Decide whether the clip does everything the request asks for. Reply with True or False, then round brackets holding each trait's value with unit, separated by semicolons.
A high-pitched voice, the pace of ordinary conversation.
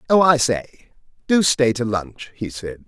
False (120 Hz; 190 wpm)